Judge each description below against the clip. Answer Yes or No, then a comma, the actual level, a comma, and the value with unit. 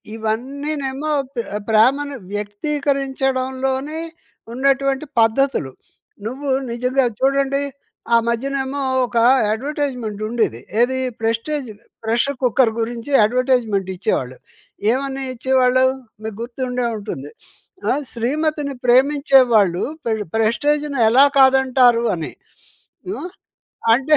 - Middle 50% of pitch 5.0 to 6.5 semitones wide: No, average, 3.2 semitones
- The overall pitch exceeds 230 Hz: Yes, very high, 260 Hz